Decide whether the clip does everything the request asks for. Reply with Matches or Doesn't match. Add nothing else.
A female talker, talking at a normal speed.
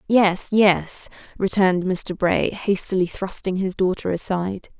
Doesn't match